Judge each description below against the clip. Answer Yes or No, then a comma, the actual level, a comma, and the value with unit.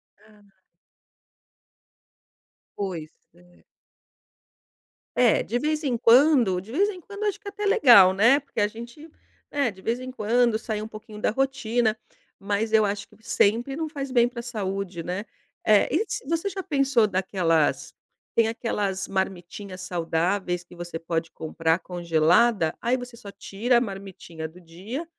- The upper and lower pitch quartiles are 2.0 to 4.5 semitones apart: No, average, 5.2 semitones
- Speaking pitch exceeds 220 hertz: No, high, 215 Hz